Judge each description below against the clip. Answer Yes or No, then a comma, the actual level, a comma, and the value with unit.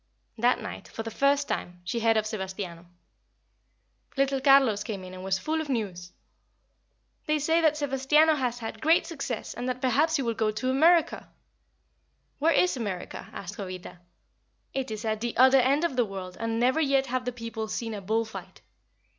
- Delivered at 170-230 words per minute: Yes, average, 185 wpm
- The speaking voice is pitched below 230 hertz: No, high, 240 Hz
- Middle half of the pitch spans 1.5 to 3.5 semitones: No, average, 4.4 semitones